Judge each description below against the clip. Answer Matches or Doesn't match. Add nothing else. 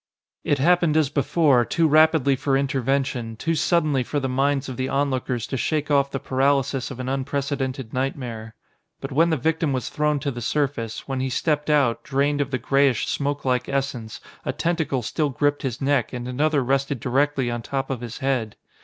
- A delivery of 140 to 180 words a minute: Doesn't match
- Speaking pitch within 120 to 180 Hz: Matches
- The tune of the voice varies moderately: Doesn't match